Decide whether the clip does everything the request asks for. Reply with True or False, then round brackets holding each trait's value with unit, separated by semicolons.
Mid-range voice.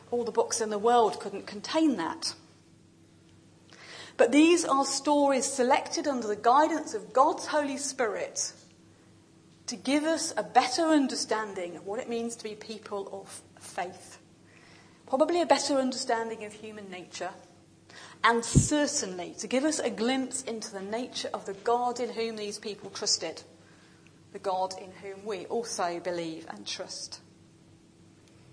False (235 Hz)